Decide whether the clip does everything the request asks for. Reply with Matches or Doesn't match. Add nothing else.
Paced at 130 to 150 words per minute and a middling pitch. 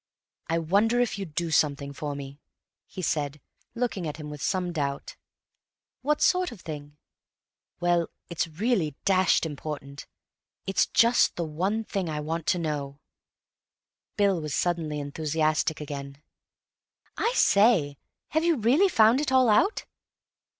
Matches